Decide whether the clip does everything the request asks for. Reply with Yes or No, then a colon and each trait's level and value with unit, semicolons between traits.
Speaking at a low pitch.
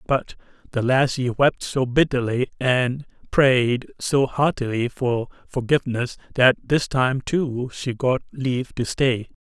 Yes: low, 130 Hz